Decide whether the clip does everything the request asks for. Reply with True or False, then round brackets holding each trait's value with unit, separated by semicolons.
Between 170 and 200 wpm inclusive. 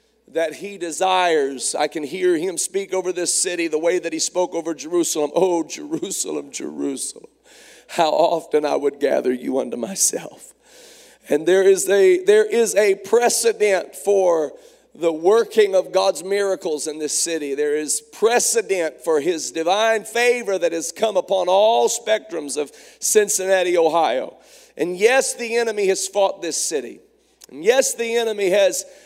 False (155 wpm)